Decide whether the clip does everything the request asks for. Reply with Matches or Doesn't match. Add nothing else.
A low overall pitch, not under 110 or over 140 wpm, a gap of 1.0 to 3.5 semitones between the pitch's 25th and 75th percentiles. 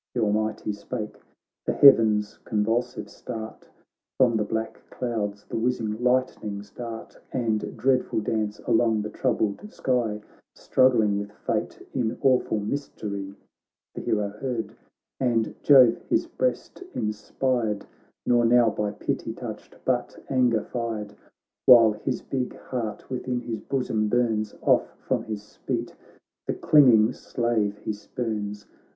Matches